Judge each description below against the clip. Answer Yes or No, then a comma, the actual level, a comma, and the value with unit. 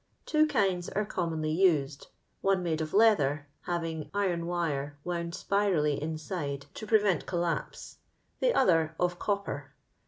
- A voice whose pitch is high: No, medium, 170 Hz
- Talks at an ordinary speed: No, slow, 120 wpm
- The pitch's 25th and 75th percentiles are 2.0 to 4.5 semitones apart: Yes, average, 4.0 semitones